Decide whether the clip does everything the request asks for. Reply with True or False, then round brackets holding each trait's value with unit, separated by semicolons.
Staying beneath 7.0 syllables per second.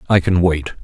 True (5.8 syllables/s)